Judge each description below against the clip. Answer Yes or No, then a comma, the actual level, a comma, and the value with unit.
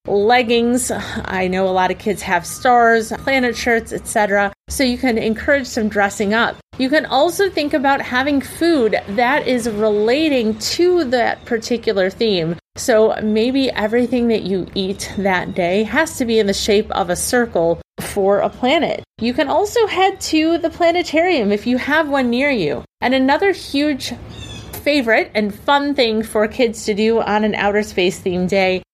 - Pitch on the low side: No, high, 230 Hz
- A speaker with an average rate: Yes, average, 170 wpm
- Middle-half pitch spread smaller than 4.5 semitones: No, average, 4.9 semitones